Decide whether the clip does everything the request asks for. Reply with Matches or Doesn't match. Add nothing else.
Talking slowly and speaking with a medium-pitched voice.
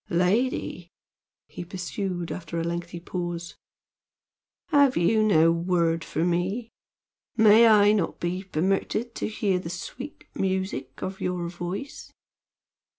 Matches